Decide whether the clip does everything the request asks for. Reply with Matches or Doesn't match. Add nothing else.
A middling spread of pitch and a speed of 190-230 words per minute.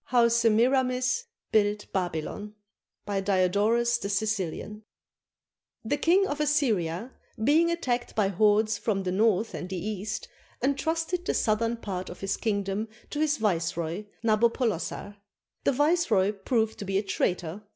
Doesn't match